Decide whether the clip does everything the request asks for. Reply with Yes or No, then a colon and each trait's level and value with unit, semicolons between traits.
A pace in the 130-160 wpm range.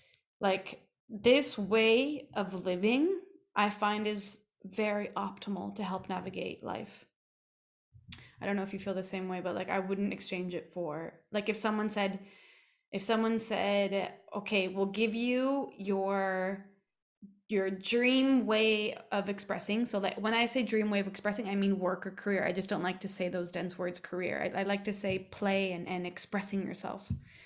No: average, 175 wpm